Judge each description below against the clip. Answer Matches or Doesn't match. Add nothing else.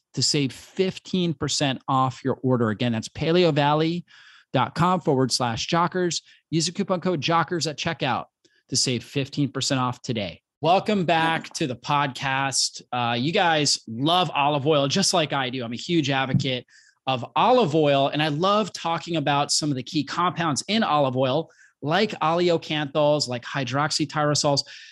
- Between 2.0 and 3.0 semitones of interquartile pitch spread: Doesn't match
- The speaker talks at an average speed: Matches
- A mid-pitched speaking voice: Matches